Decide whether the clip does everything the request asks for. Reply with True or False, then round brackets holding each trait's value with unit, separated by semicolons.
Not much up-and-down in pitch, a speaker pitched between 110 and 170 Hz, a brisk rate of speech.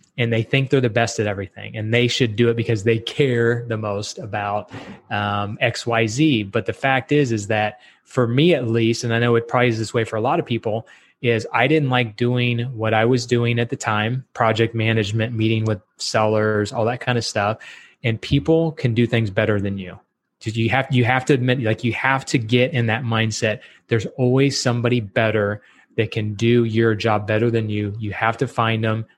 True (2.1 semitones; 115 Hz; 220 wpm)